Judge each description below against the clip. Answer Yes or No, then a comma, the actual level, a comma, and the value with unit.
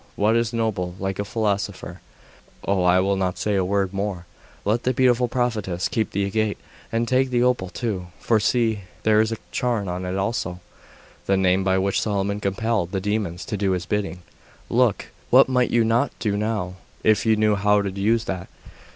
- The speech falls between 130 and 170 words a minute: No, average, 195 wpm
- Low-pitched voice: Yes, low, 105 Hz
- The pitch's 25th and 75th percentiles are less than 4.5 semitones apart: Yes, average, 3.1 semitones